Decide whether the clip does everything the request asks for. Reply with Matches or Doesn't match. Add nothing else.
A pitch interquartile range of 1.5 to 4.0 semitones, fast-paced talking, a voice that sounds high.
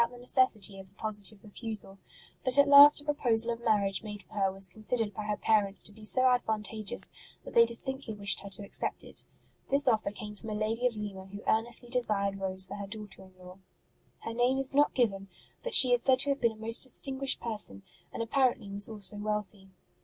Matches